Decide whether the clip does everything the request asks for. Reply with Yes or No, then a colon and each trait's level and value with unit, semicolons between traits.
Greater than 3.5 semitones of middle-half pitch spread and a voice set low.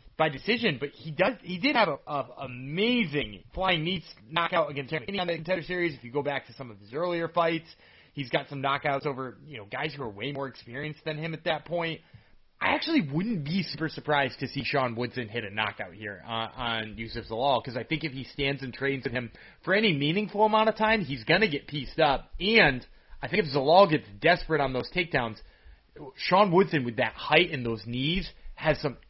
No: average, 5.2 semitones; medium, 145 Hz